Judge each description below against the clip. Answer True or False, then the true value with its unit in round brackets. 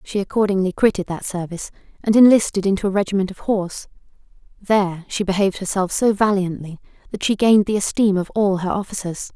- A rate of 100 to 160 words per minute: False (175 wpm)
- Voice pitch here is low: False (195 Hz)